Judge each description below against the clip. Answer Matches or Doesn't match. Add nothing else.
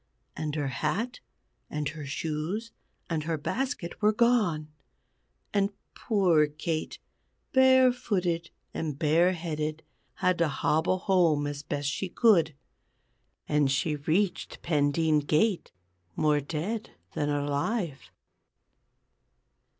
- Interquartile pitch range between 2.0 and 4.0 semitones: Doesn't match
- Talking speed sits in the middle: Doesn't match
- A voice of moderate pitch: Matches